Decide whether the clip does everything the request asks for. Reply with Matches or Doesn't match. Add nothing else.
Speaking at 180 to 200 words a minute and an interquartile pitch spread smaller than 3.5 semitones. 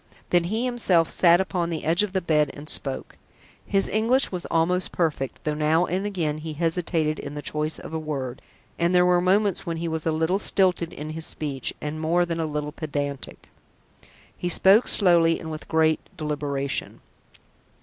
Matches